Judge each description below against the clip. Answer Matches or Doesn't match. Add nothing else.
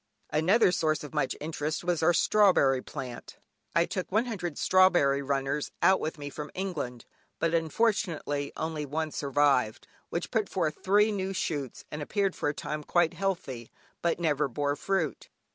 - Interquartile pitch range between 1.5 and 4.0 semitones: Doesn't match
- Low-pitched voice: Doesn't match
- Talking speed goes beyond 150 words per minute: Matches